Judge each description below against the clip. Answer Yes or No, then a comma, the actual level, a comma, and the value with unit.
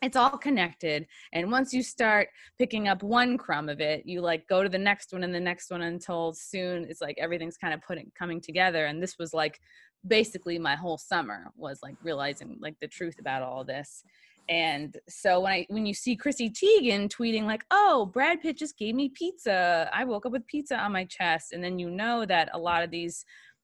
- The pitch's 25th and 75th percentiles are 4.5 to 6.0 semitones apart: Yes, wide, 5.6 semitones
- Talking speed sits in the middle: No, fast, 220 wpm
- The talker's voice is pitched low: No, medium, 185 Hz